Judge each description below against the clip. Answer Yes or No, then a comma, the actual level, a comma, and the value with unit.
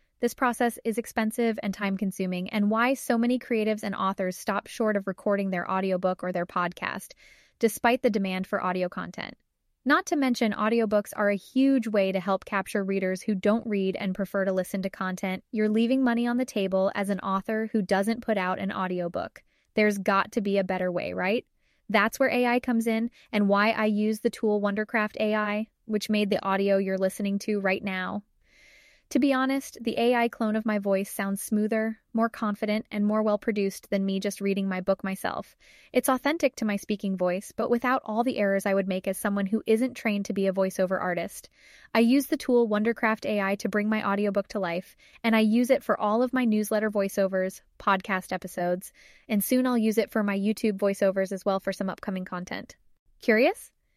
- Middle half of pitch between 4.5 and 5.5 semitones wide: No, average, 2.9 semitones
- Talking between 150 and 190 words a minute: No, fast, 205 wpm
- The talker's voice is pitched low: No, high, 210 Hz